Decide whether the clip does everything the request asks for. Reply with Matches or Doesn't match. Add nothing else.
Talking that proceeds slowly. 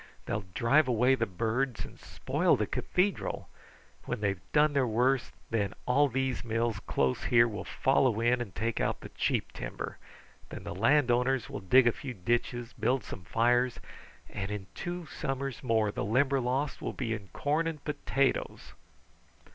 Doesn't match